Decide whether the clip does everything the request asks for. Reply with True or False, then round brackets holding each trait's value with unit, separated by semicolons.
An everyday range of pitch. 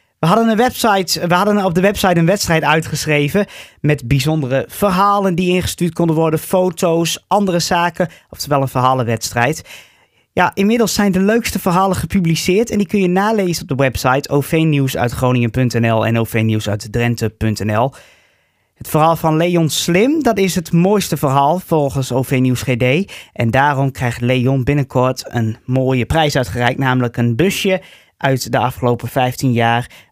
False (6.3 semitones)